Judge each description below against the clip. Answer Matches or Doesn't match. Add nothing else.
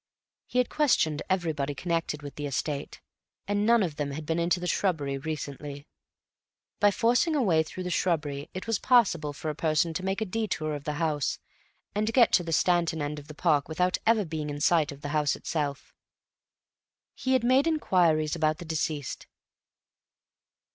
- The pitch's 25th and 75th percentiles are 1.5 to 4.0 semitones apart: Doesn't match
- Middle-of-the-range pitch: Matches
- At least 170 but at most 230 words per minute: Matches